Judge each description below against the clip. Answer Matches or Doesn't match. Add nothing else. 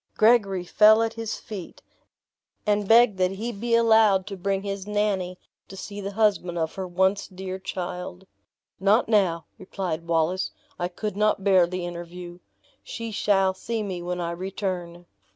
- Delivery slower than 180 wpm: Matches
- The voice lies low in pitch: Doesn't match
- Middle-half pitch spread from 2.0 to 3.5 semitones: Matches